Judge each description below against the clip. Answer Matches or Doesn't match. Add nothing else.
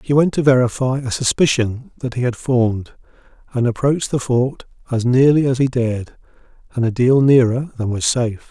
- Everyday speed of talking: Matches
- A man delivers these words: Matches